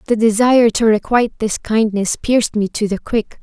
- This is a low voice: No, high, 220 Hz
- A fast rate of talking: No, average, 195 wpm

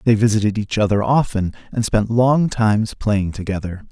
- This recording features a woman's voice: No, male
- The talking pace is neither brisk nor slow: Yes, average, 170 wpm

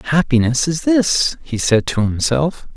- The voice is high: No, medium, 140 Hz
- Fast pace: No, average, 150 wpm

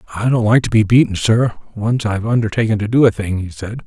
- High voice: No, low, 110 Hz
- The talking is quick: Yes, fast, 250 wpm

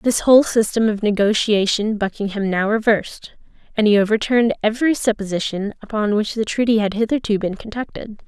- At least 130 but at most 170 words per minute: Yes, average, 150 wpm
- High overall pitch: Yes, high, 215 Hz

